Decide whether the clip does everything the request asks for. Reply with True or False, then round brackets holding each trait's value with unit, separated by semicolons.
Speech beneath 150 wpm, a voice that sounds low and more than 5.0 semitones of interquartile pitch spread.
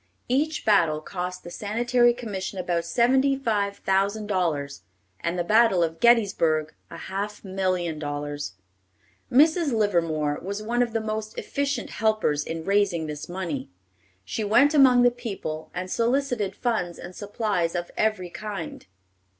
False (140 wpm; 200 Hz; 5.4 semitones)